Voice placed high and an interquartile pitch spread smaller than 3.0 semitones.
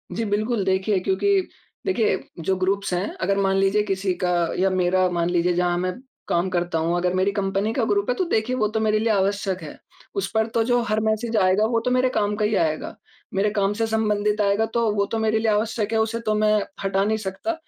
Yes: high, 205 Hz; narrow, 2.6 semitones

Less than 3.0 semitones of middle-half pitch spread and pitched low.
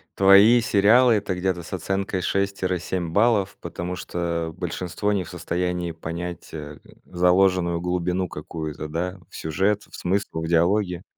Yes: narrow, 2.4 semitones; very low, 90 Hz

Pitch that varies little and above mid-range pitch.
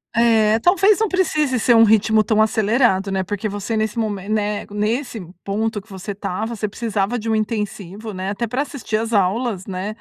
Yes: narrow, 2.3 semitones; high, 215 Hz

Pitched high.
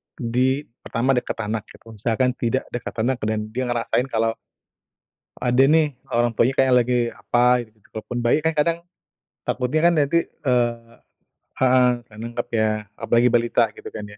No: low, 120 Hz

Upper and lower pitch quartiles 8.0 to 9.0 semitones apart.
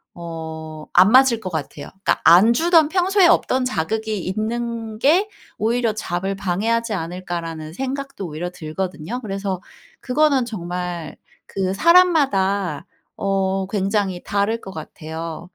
No: average, 5.3 semitones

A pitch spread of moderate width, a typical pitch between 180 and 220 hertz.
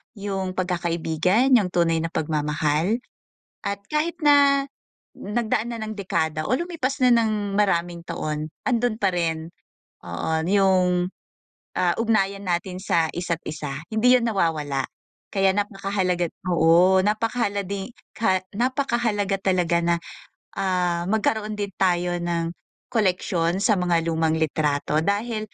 Yes: average, 4.1 semitones; medium, 185 Hz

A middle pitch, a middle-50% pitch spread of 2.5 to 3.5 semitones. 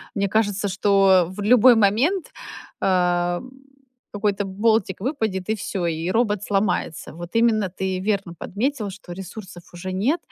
No: high, 200 Hz; average, 2.8 semitones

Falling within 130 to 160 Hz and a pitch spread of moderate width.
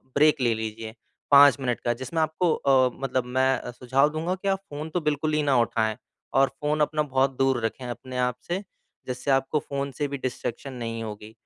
Yes: low, 135 Hz; average, 3.4 semitones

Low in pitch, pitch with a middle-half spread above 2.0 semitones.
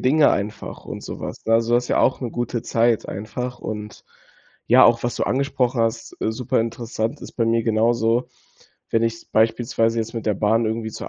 No: low, 115 Hz; narrow, 1.3 semitones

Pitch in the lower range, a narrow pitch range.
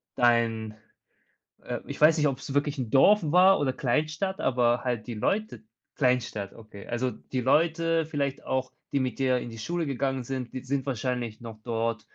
No: low, 130 Hz; average, 3.9 semitones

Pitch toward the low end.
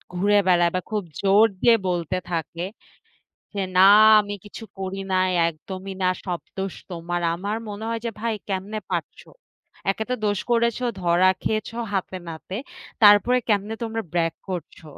No: high, 195 Hz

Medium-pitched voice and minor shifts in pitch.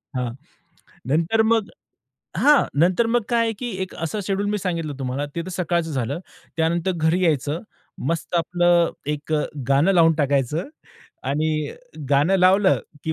No: medium, 165 Hz; average, 3.9 semitones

